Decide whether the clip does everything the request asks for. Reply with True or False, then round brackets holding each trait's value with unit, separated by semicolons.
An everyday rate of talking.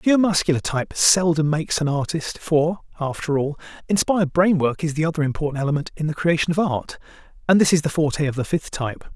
False (215 wpm)